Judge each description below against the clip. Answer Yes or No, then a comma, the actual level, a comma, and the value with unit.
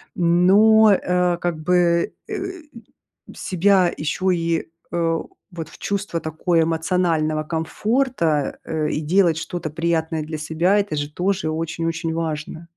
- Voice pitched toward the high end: No, medium, 170 Hz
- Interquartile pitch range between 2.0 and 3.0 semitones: Yes, narrow, 2.4 semitones